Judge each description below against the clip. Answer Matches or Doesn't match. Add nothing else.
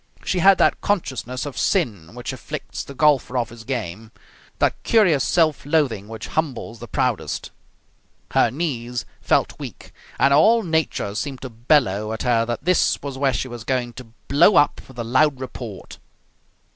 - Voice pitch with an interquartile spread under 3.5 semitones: Doesn't match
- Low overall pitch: Matches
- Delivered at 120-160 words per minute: Doesn't match